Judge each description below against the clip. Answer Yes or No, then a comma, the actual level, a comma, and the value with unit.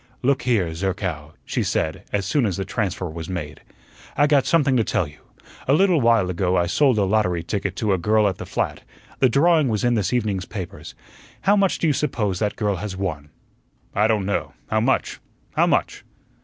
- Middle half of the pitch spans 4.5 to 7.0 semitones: Yes, average, 5.1 semitones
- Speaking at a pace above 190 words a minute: Yes, fast, 205 wpm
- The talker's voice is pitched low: Yes, low, 105 Hz